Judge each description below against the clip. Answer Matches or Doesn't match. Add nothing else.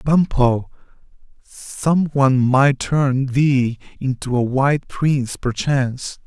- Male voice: Matches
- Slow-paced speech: Matches